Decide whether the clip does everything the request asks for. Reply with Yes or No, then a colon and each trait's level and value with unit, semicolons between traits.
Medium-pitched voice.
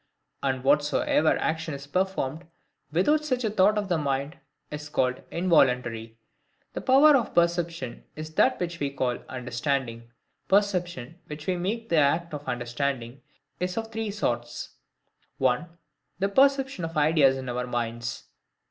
Yes: medium, 155 Hz